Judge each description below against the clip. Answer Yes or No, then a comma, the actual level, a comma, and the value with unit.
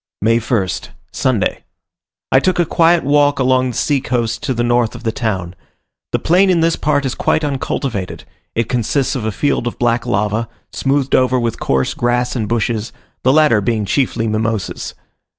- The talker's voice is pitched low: Yes, low, 120 Hz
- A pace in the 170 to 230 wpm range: Yes, average, 180 wpm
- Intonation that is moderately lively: Yes, average, 3.8 semitones